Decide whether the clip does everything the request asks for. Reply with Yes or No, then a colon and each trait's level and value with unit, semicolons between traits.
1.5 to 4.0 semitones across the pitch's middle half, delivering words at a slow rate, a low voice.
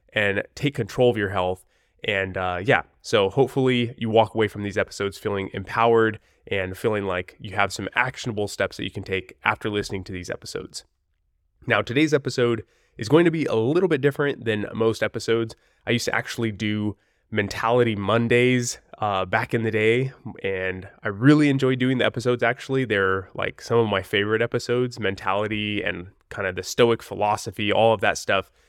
No: average, 3.6 semitones; average, 185 wpm; low, 110 Hz